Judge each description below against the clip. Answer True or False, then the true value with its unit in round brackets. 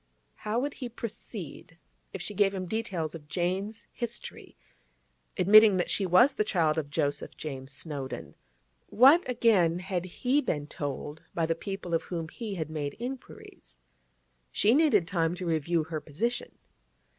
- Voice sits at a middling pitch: True (180 Hz)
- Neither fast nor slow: True (155 wpm)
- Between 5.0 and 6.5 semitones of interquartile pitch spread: True (5.5 semitones)